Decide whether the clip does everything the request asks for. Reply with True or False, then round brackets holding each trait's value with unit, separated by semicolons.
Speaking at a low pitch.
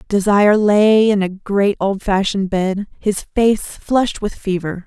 False (200 Hz)